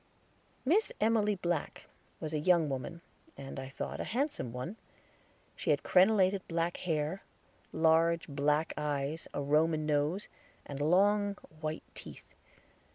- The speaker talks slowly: Yes, slow, 130 wpm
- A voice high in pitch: No, medium, 165 Hz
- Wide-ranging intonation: No, average, 4.3 semitones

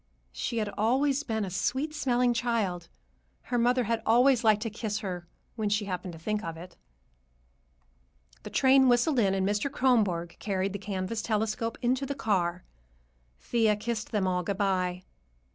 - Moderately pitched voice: No, high, 215 Hz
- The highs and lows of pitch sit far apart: No, average, 4.1 semitones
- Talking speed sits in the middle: Yes, average, 165 wpm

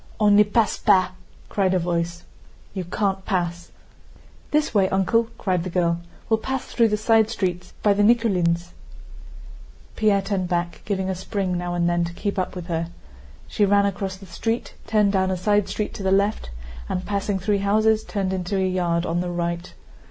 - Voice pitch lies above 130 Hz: Yes, high, 190 Hz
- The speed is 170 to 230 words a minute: Yes, average, 195 wpm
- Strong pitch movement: No, average, 2.8 semitones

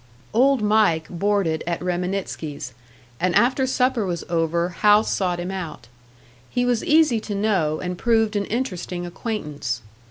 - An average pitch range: Yes, average, 4.5 semitones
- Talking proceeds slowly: No, average, 145 wpm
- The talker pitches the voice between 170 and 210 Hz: Yes, high, 190 Hz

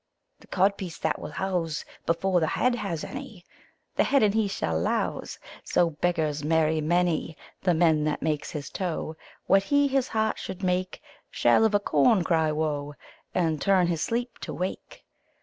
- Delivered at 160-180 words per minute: Yes, average, 170 wpm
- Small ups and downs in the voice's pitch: No, average, 4.0 semitones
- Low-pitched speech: No, medium, 175 Hz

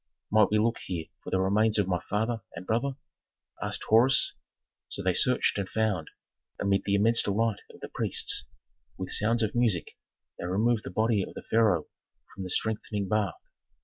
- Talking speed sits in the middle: Yes, average, 180 wpm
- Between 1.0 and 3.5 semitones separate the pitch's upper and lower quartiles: Yes, average, 2.8 semitones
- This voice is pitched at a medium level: No, low, 105 Hz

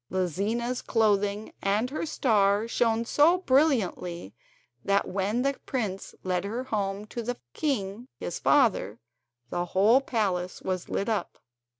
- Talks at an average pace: No, slow, 130 wpm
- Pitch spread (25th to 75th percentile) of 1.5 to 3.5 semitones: No, average, 4.1 semitones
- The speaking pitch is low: No, high, 210 Hz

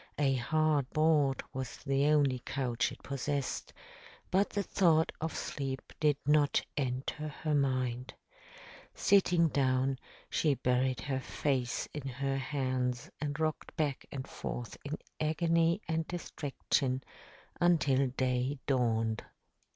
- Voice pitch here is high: No, medium, 140 Hz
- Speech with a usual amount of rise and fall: Yes, average, 3.0 semitones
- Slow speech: Yes, slow, 120 wpm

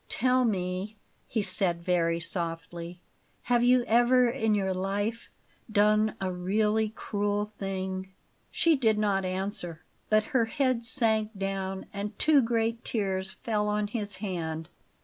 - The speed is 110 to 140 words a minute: Yes, slow, 135 wpm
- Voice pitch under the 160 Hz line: No, high, 205 Hz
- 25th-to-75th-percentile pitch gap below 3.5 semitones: Yes, average, 3.1 semitones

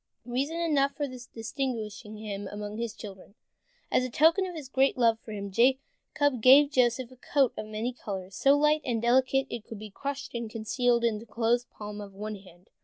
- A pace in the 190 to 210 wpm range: Yes, average, 200 wpm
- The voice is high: Yes, high, 235 Hz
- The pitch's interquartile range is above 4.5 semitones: No, average, 4.2 semitones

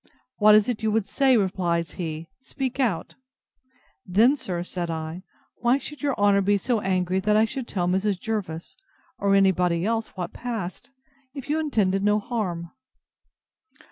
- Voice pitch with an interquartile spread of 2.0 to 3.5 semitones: No, average, 4.3 semitones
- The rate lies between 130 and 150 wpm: No, average, 160 wpm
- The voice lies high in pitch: Yes, high, 200 Hz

